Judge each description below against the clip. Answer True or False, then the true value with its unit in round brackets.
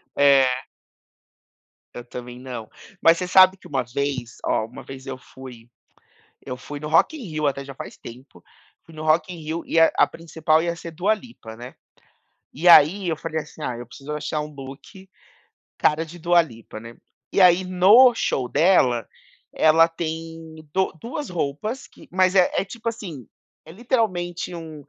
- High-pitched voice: False (160 Hz)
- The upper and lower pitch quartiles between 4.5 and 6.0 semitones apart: True (4.9 semitones)